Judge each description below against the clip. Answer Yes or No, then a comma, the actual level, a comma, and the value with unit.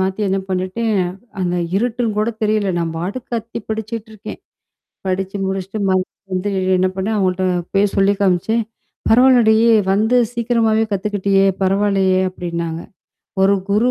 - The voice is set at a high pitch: Yes, high, 200 Hz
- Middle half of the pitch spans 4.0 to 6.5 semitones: No, average, 2.8 semitones